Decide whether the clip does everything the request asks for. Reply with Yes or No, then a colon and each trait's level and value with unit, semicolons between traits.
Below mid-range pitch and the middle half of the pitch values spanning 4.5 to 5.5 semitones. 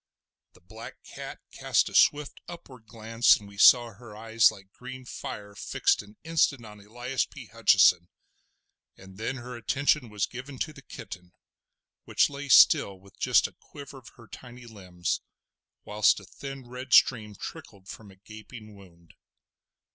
No: low, 115 Hz; average, 4.0 semitones